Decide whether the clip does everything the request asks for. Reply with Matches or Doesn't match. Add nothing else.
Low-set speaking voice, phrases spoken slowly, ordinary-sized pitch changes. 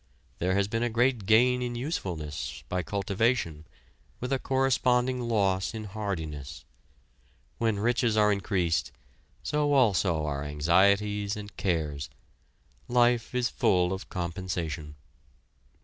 Doesn't match